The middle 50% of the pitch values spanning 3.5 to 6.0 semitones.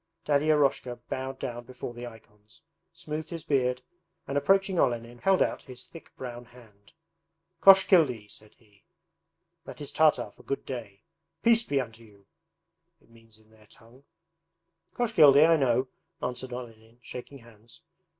Yes: average, 4.2 semitones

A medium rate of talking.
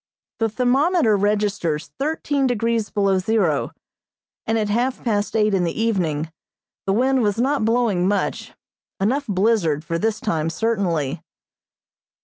No: slow, 130 wpm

